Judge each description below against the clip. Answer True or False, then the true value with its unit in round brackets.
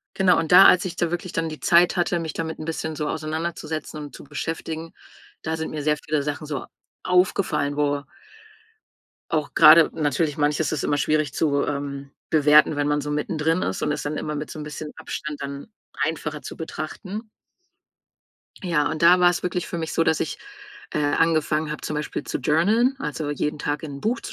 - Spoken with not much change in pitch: True (1.9 semitones)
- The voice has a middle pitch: True (155 Hz)